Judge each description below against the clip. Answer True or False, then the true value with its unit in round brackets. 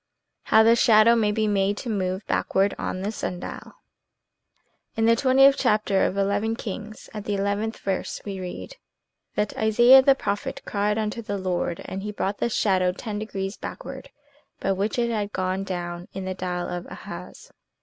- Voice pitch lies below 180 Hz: False (205 Hz)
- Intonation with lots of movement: False (2.5 semitones)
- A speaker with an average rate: True (180 wpm)